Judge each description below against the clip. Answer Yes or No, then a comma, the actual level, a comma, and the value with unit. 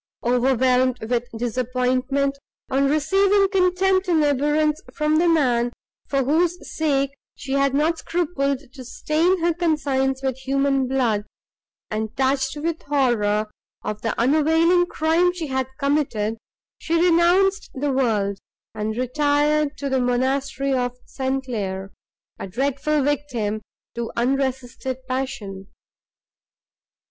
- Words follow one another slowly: Yes, slow, 120 wpm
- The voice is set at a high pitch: Yes, very high, 275 Hz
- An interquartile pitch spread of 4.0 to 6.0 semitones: No, average, 3.6 semitones